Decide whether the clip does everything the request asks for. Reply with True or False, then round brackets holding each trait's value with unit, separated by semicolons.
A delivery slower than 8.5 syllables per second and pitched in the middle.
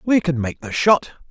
True (4.9 syllables/s; 155 Hz)